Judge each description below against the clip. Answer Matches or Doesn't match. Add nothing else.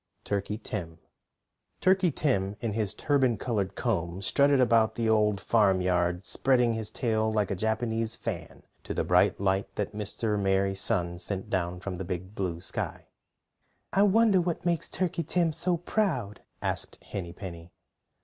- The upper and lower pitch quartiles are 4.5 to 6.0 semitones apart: Matches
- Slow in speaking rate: Doesn't match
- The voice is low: Matches